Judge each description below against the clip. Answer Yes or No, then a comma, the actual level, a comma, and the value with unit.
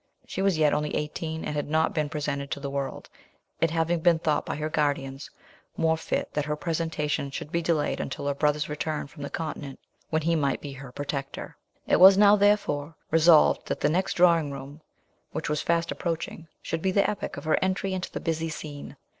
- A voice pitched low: No, medium, 155 Hz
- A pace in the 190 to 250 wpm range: Yes, fast, 205 wpm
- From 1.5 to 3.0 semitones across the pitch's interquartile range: Yes, narrow, 2.4 semitones